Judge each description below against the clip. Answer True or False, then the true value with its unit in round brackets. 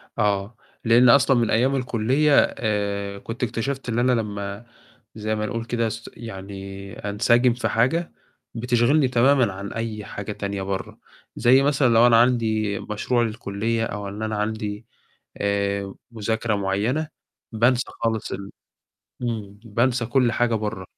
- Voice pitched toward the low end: True (115 Hz)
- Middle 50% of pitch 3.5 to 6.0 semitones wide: False (3.0 semitones)